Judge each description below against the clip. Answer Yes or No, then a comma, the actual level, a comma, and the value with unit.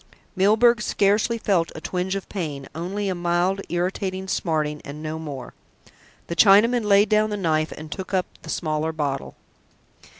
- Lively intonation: No, average, 4.3 semitones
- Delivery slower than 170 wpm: Yes, average, 160 wpm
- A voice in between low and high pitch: Yes, medium, 180 Hz